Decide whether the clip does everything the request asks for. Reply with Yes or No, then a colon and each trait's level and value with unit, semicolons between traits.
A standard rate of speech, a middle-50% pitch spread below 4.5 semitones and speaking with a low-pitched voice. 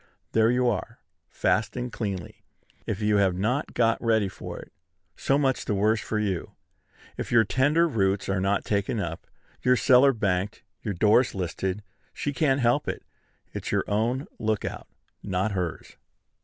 Yes: average, 160 wpm; average, 4.1 semitones; low, 110 Hz